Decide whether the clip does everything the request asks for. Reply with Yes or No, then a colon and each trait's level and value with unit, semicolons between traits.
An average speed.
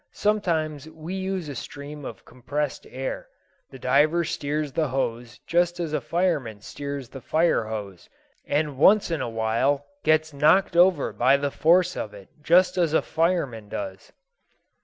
Yes: average, 160 wpm